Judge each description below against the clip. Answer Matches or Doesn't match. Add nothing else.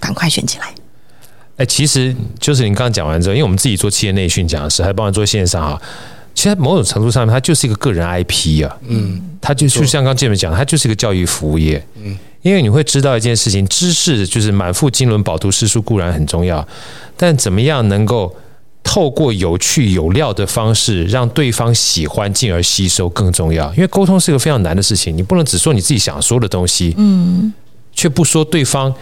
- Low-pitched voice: Matches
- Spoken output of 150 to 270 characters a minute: Doesn't match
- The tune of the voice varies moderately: Doesn't match